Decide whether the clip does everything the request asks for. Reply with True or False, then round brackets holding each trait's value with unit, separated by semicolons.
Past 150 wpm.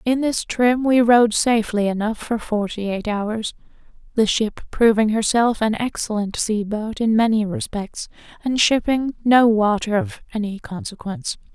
False (145 wpm)